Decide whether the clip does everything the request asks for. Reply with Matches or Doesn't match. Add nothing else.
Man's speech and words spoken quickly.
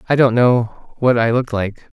Matches